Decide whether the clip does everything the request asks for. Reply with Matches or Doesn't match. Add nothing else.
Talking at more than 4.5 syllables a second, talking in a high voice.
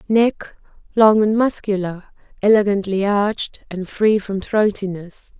Doesn't match